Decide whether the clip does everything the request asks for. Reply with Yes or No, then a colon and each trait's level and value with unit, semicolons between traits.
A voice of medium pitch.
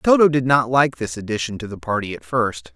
No: low, 115 Hz